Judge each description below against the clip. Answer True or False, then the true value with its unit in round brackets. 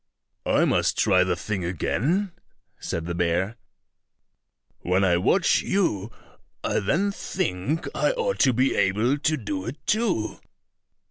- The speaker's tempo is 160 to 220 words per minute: False (135 wpm)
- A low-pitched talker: True (110 Hz)